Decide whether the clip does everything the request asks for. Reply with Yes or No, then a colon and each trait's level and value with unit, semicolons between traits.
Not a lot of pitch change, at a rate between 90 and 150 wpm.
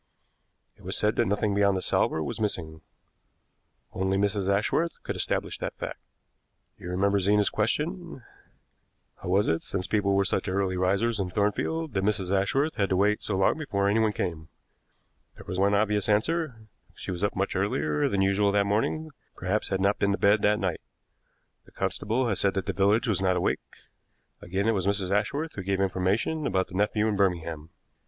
No: narrow, 2.0 semitones; average, 190 wpm